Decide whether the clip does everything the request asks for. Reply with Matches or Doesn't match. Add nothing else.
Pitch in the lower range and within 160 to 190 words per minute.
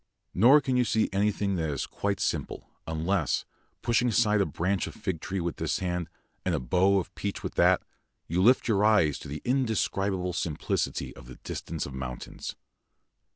Matches